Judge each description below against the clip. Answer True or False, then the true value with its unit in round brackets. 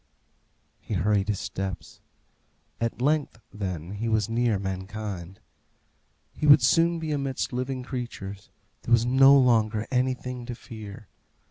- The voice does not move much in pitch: False (4.3 semitones)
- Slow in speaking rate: True (130 wpm)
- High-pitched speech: False (115 Hz)